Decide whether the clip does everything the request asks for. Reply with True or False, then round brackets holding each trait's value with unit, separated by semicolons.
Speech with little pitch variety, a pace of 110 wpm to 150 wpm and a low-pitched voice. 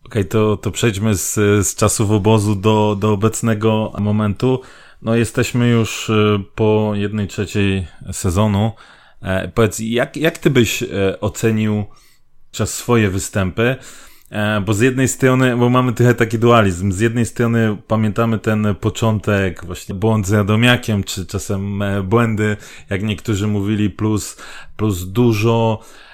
True (2.1 semitones; 130 wpm; 110 Hz)